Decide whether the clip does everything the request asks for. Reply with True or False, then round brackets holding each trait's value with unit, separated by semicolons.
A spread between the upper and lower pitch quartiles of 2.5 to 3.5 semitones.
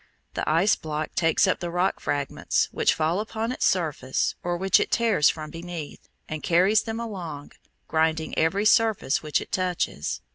False (4.1 semitones)